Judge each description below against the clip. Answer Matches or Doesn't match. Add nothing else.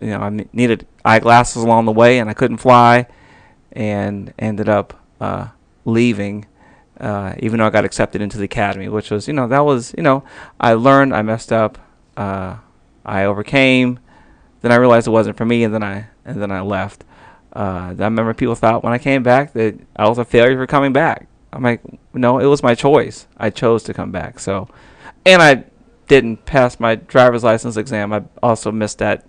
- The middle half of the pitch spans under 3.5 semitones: Matches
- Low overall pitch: Matches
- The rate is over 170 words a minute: Matches